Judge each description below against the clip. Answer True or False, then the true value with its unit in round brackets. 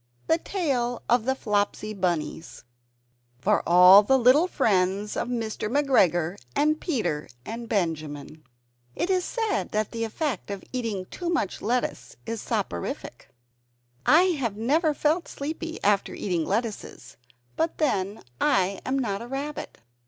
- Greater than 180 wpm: False (135 wpm)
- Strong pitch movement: True (6.4 semitones)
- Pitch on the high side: True (225 Hz)